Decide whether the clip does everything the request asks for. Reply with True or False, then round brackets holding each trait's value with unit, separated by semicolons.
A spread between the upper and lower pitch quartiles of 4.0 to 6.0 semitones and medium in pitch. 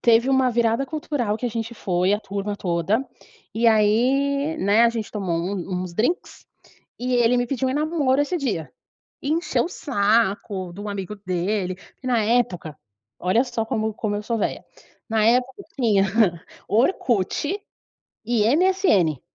False (4.5 semitones; 225 Hz)